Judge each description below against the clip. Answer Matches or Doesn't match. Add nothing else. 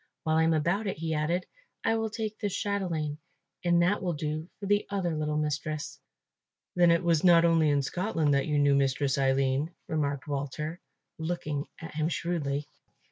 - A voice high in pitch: Doesn't match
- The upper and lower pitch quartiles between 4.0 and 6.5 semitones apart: Doesn't match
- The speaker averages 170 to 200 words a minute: Matches